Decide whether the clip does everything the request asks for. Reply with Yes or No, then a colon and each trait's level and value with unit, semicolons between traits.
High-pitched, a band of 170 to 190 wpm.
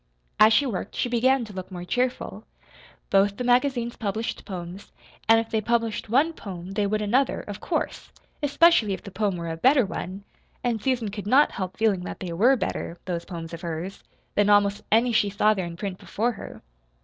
No: high, 210 Hz; average, 200 wpm